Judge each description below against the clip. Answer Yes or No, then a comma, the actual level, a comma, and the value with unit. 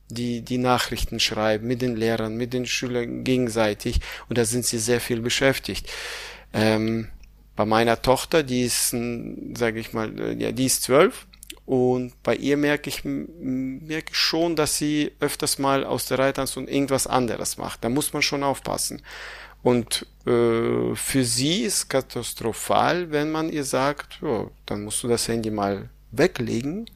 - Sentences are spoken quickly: No, average, 160 wpm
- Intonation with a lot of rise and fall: No, average, 3.3 semitones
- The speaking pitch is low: Yes, low, 125 Hz